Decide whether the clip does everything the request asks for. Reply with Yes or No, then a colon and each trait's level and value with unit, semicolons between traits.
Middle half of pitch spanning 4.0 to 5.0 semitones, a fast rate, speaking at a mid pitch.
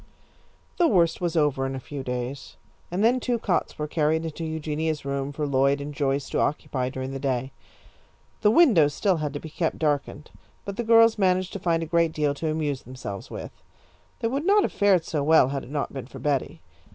Yes: average, 4.3 semitones; fast, 210 wpm; medium, 155 Hz